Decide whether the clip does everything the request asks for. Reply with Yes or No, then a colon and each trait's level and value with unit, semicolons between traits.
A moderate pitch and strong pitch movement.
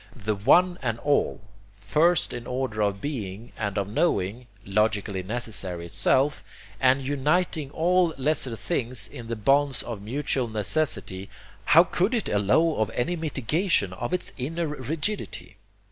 No: low, 125 Hz; wide, 6.8 semitones